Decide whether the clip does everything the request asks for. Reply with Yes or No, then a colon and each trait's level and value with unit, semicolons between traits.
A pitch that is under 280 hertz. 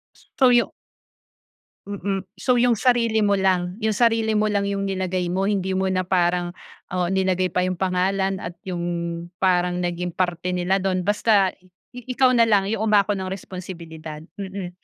Yes: high, 190 Hz